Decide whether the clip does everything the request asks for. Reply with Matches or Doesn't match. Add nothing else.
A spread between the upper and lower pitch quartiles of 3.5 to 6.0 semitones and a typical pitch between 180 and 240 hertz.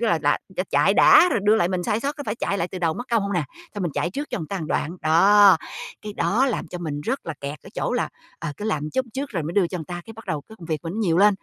Matches